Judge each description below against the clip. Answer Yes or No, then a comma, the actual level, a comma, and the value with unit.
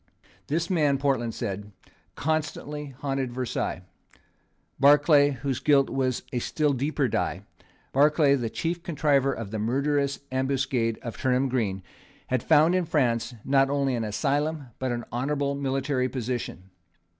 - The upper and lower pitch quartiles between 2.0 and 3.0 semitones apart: Yes, average, 2.7 semitones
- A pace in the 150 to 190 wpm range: No, average, 140 wpm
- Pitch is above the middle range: No, low, 135 Hz